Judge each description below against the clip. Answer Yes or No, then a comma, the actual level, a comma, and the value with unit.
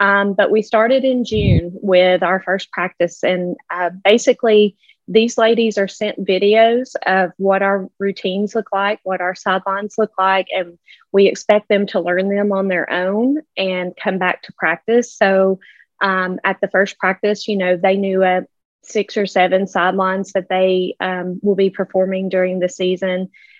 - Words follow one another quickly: No, average, 175 wpm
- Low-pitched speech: No, high, 195 Hz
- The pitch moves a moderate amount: No, narrow, 2.0 semitones